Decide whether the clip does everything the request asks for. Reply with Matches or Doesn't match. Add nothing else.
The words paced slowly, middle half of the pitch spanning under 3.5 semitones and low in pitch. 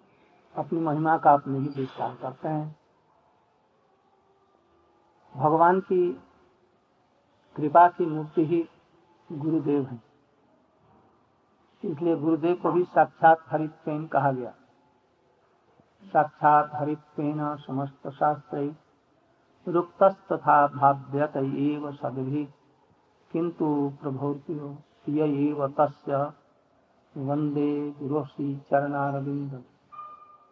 Doesn't match